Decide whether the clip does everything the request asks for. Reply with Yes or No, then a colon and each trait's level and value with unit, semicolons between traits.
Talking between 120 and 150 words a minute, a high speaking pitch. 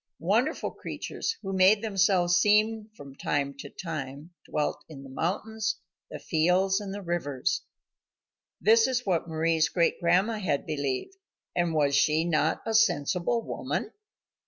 No: average, 140 wpm; medium, 175 Hz